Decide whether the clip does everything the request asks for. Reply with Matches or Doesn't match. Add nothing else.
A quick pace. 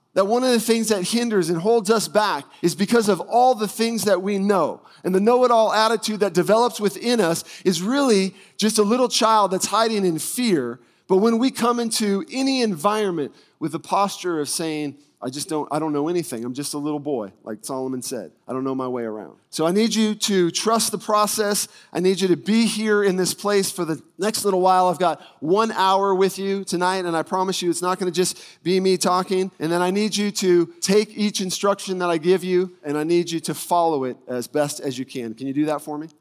Matches